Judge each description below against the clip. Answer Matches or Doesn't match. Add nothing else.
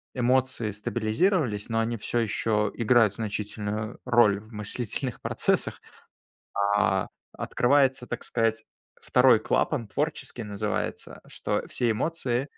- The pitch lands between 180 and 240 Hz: Doesn't match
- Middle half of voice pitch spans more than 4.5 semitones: Doesn't match